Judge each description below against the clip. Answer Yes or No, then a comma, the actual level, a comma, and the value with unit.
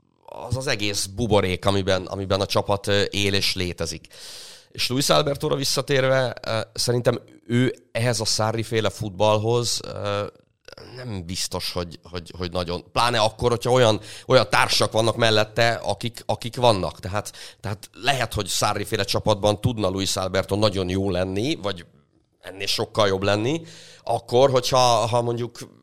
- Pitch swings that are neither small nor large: Yes, average, 3.5 semitones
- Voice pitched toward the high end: No, low, 110 Hz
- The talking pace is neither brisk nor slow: Yes, average, 135 wpm